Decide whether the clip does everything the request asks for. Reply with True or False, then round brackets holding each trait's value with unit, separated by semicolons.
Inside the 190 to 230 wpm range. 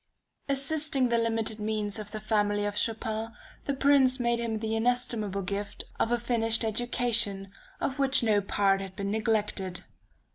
False (155 wpm)